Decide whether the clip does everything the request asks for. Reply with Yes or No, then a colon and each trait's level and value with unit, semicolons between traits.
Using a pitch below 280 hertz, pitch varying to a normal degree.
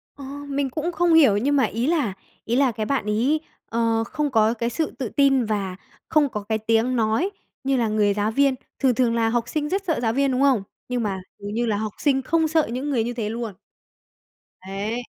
Yes: high, 240 Hz; average, 4.2 semitones